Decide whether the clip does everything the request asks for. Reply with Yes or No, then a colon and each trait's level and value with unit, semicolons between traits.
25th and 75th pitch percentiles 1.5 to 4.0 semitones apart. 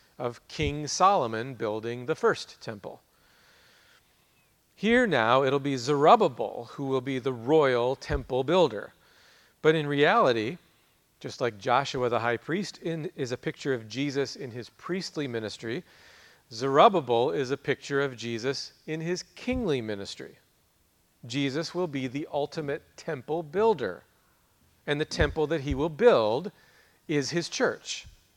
No: average, 4.4 semitones